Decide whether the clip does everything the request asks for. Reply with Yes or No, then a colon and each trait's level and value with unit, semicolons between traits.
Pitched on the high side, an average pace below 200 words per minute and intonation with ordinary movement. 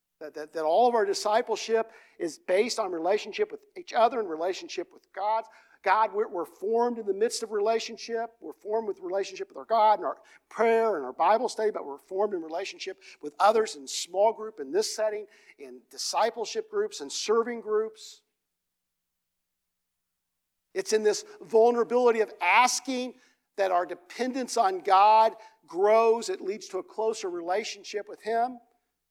Yes: high, 225 Hz; average, 165 wpm; average, 4.3 semitones